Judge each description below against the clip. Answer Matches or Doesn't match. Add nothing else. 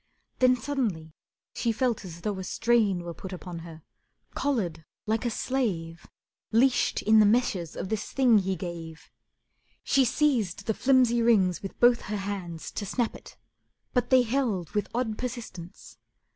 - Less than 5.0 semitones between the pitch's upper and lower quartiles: Doesn't match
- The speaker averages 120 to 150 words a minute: Doesn't match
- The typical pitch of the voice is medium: Doesn't match